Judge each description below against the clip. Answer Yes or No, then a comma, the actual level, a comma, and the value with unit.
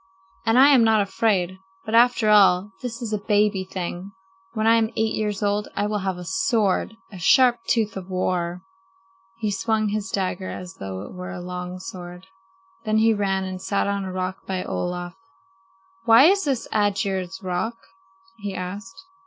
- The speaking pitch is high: Yes, high, 200 Hz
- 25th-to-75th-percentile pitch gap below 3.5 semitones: Yes, average, 3.1 semitones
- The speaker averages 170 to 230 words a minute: Yes, average, 180 wpm